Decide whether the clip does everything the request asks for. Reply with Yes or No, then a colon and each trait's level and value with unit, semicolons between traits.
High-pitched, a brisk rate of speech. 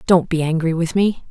No: medium, 170 Hz; fast, 230 wpm